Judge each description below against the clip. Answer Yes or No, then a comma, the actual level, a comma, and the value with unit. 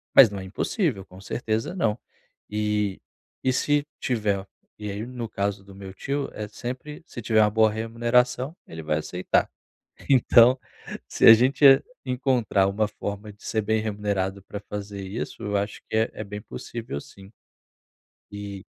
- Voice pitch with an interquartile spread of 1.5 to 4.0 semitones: Yes, average, 3.3 semitones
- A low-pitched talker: Yes, low, 105 Hz